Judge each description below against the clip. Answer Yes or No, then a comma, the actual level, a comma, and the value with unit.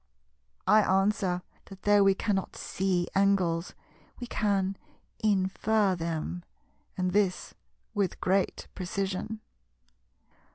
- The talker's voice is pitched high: Yes, high, 195 Hz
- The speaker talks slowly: Yes, slow, 95 wpm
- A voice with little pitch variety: Yes, narrow, 2.0 semitones